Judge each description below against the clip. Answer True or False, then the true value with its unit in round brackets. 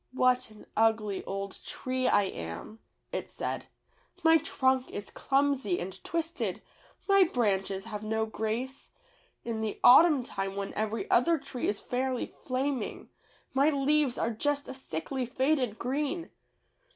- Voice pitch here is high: True (250 Hz)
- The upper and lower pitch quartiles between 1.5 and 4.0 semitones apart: False (4.5 semitones)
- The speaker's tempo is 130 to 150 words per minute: True (140 wpm)